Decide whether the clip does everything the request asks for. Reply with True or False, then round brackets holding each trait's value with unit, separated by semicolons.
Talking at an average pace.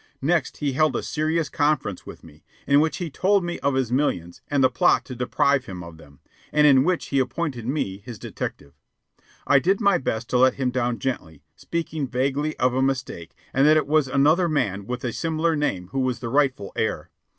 False (210 wpm)